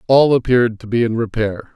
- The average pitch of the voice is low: Yes, low, 115 Hz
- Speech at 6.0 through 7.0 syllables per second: Yes, 6.2 syllables/s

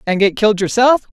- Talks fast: Yes, fast, 210 wpm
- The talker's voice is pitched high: Yes, high, 215 Hz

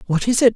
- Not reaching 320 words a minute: No, fast, 325 wpm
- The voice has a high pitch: Yes, high, 215 Hz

